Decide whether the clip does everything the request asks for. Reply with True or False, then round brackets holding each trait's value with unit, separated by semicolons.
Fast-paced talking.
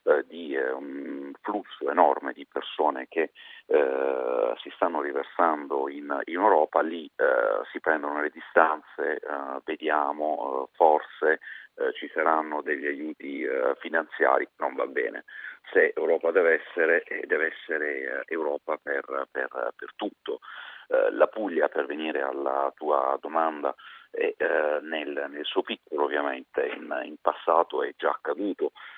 False (135 wpm)